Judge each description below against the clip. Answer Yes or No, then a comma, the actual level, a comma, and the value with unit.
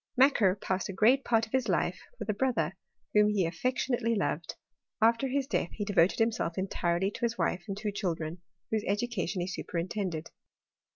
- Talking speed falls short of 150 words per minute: No, average, 185 wpm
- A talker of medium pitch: No, high, 205 Hz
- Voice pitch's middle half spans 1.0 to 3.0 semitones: No, average, 4.4 semitones